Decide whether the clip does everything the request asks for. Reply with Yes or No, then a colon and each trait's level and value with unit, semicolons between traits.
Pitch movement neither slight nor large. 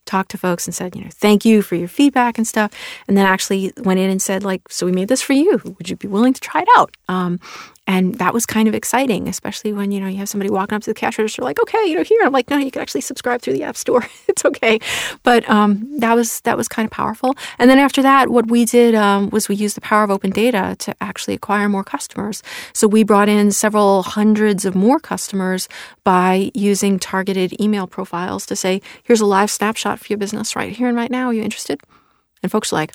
Yes: average, 3.7 semitones